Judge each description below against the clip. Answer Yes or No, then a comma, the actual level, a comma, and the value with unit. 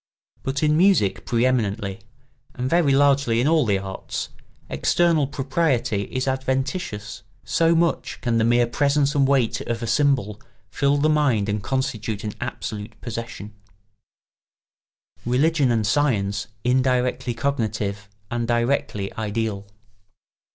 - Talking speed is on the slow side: Yes, slow, 130 wpm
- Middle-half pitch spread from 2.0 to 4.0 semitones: No, average, 4.6 semitones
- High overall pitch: No, low, 125 Hz